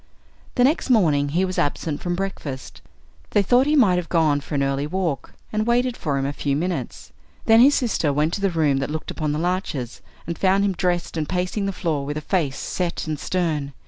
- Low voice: No, medium, 170 Hz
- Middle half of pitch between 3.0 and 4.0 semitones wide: No, average, 4.9 semitones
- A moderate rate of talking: No, fast, 220 wpm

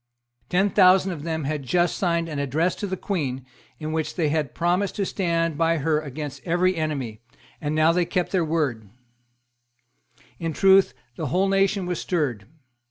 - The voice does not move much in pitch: No, average, 3.3 semitones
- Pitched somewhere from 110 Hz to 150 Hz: No, medium, 165 Hz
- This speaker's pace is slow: No, average, 170 wpm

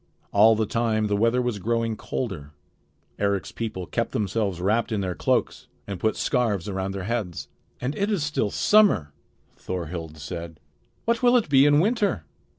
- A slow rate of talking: No, average, 165 wpm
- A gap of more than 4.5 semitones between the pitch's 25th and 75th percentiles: Yes, average, 5.1 semitones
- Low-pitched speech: Yes, low, 110 Hz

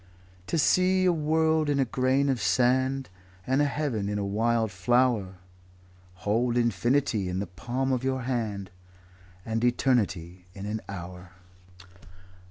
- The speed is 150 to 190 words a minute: No, average, 140 wpm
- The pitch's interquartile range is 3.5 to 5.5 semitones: Yes, average, 5.0 semitones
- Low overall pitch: Yes, low, 120 Hz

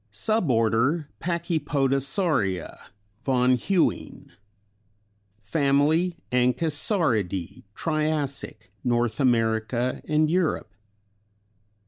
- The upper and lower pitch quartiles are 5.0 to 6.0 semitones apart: Yes, average, 5.3 semitones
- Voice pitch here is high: No, low, 135 Hz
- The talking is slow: Yes, slow, 55 wpm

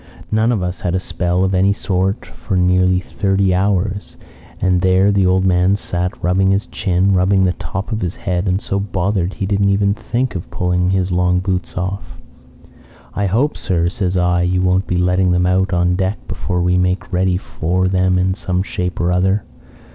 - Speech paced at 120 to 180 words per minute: No, average, 195 wpm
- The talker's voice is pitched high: No, very low, 95 Hz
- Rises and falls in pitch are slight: Yes, narrow, 1.4 semitones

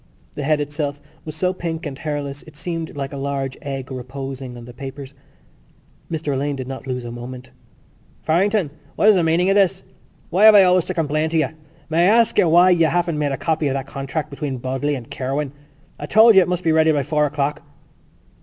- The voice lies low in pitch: No, medium, 150 Hz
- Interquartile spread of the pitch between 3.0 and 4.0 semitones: Yes, average, 3.7 semitones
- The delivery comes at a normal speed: No, fast, 220 wpm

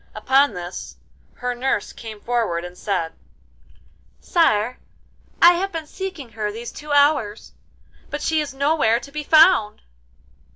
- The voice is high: Yes, very high, 250 Hz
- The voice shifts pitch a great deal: Yes, wide, 6.2 semitones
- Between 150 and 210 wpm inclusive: No, slow, 135 wpm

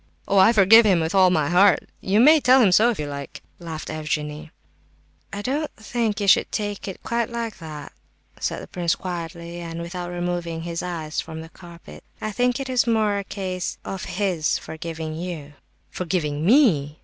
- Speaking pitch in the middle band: Yes, medium, 180 Hz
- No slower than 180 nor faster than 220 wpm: Yes, average, 185 wpm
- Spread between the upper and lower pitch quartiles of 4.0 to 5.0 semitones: Yes, average, 4.3 semitones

